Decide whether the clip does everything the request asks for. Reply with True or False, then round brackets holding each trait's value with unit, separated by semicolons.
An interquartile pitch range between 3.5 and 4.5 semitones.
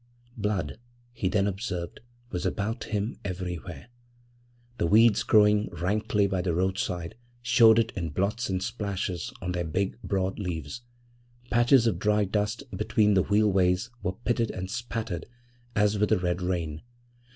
False (3.1 semitones)